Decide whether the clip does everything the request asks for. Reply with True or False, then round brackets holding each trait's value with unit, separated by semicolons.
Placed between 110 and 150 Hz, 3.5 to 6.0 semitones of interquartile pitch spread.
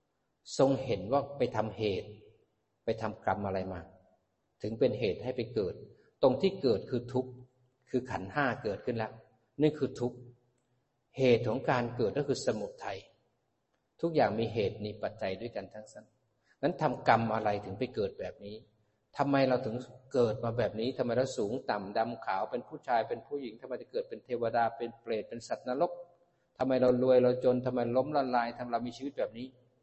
False (125 Hz; 2.7 semitones)